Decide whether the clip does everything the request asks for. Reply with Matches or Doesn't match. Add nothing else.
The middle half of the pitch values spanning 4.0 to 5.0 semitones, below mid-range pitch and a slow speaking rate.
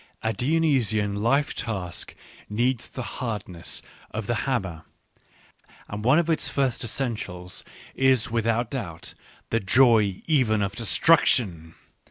Matches